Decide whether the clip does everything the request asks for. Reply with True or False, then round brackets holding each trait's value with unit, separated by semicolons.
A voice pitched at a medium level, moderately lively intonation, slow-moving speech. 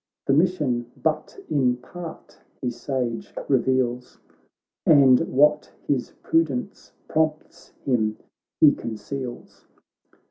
False (130 Hz; 3.7 semitones; 95 wpm)